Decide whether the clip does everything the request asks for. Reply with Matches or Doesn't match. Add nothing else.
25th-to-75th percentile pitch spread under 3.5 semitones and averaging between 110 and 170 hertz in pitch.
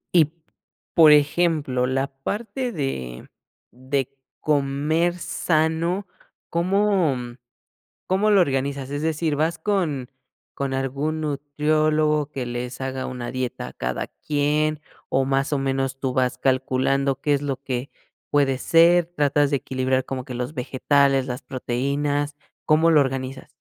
Matches